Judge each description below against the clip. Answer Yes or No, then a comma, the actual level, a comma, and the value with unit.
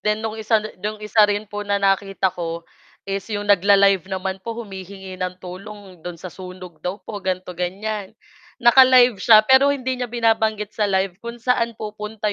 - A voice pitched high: Yes, high, 205 Hz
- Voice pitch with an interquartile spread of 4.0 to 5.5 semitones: No, average, 2.7 semitones